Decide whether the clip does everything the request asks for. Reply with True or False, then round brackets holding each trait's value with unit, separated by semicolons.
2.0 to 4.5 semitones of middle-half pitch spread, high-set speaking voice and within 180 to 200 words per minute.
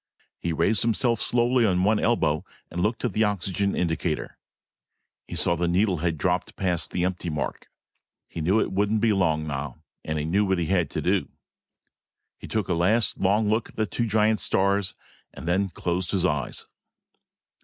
False (3.8 semitones; 95 Hz; 185 wpm)